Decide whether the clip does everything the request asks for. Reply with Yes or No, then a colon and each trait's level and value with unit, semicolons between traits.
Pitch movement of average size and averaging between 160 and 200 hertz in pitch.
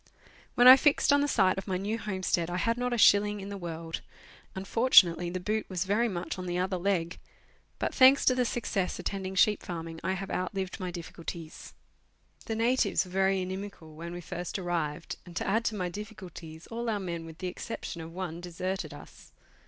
Yes: average, 3.2 semitones; medium, 185 Hz